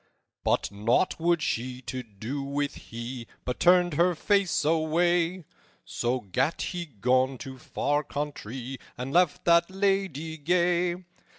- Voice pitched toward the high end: No, medium, 145 Hz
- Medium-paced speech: No, slow, 130 wpm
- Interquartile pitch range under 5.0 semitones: No, average, 5.3 semitones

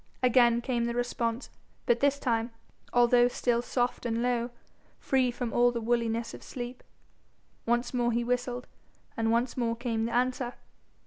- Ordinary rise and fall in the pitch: No, narrow, 1.0 semitones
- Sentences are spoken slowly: No, average, 155 wpm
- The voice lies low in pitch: No, high, 240 Hz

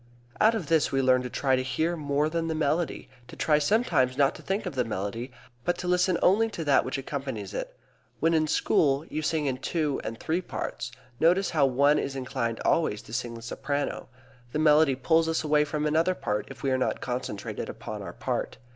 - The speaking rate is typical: No, fast, 215 wpm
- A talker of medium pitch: Yes, medium, 145 Hz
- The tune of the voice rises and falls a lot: No, average, 4.0 semitones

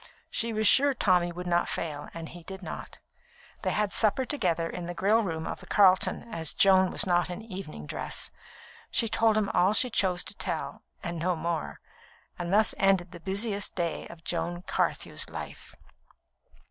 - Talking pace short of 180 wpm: No, average, 185 wpm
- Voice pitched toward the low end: No, medium, 185 Hz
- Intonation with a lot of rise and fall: No, average, 3.3 semitones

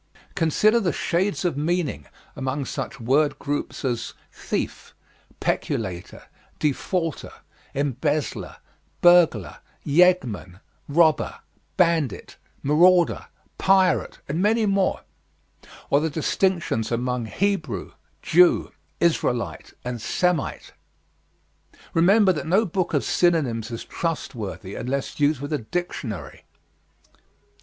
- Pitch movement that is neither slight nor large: No, wide, 6.0 semitones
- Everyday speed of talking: No, slow, 100 wpm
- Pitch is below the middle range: No, medium, 155 Hz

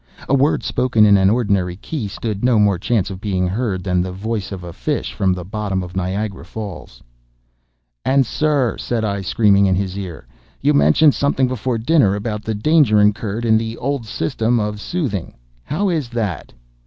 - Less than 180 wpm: No, average, 185 wpm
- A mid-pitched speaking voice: No, low, 105 Hz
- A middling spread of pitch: Yes, average, 4.1 semitones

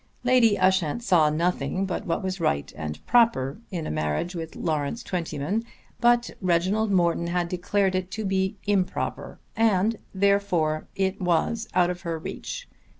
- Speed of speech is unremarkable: Yes, average, 150 wpm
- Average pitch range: Yes, average, 3.5 semitones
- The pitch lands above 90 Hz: Yes, medium, 185 Hz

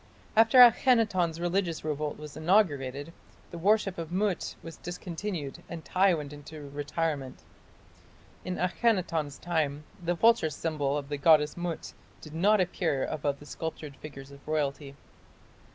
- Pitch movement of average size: Yes, average, 3.8 semitones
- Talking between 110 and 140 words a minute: Yes, slow, 135 wpm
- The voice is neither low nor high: Yes, medium, 160 Hz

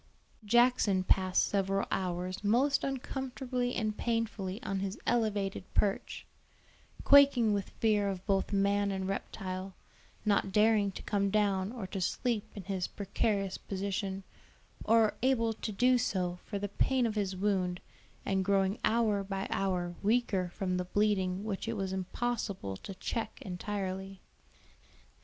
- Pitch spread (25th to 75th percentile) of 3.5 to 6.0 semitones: No, average, 2.7 semitones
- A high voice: Yes, high, 200 Hz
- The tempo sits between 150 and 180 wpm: No, average, 140 wpm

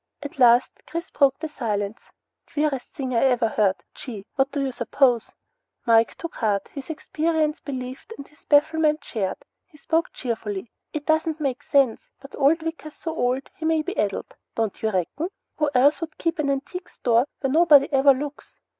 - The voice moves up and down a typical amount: Yes, average, 4.2 semitones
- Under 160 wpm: No, average, 170 wpm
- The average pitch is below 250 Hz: No, very high, 275 Hz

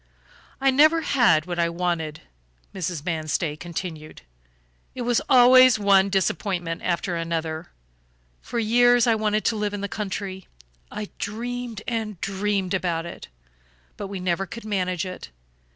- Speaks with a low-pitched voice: No, high, 195 Hz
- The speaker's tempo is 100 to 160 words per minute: Yes, average, 140 wpm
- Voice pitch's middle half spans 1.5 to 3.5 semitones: No, average, 4.6 semitones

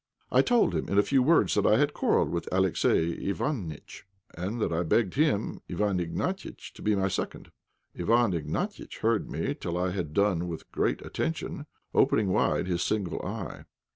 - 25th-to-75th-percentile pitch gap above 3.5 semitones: Yes, average, 4.2 semitones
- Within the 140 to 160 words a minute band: No, average, 175 wpm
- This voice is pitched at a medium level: No, very low, 95 Hz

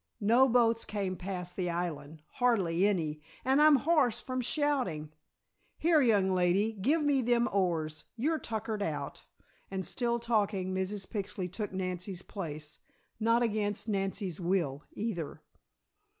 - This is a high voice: Yes, high, 200 Hz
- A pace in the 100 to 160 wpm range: Yes, slow, 135 wpm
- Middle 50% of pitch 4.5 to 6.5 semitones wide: Yes, average, 4.8 semitones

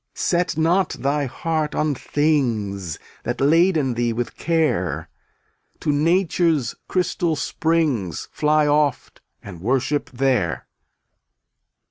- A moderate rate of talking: No, slow, 100 wpm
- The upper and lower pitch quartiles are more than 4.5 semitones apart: Yes, average, 5.0 semitones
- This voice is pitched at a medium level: Yes, medium, 145 Hz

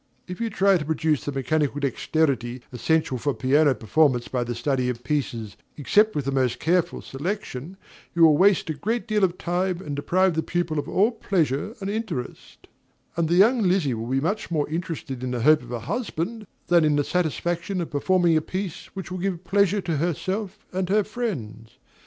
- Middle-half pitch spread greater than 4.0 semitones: Yes, wide, 5.5 semitones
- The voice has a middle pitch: Yes, medium, 160 Hz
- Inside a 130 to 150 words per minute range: No, average, 195 wpm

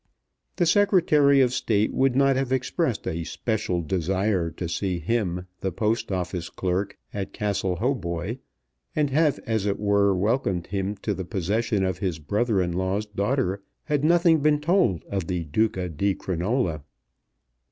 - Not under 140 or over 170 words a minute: Yes, average, 155 wpm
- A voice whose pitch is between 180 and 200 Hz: No, low, 100 Hz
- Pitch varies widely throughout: Yes, wide, 6.0 semitones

